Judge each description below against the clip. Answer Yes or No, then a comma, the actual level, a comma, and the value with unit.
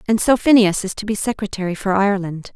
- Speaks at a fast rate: Yes, fast, 210 wpm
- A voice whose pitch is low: No, high, 205 Hz